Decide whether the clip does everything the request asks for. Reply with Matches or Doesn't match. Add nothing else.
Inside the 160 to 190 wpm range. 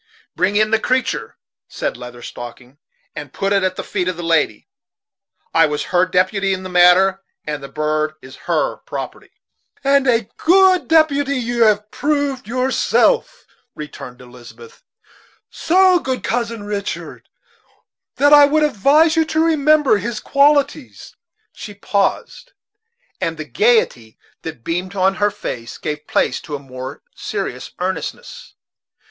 Doesn't match